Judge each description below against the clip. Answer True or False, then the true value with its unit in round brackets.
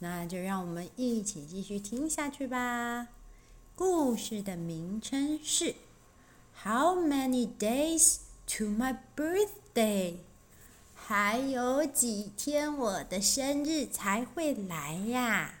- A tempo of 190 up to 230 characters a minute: True (210 characters per minute)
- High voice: True (240 Hz)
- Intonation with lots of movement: True (6.0 semitones)